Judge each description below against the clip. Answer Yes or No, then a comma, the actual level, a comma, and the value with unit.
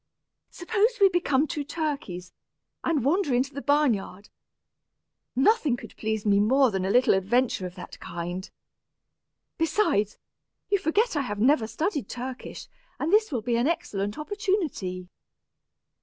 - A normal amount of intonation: No, wide, 8.0 semitones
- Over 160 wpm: No, average, 140 wpm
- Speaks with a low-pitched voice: No, very high, 265 Hz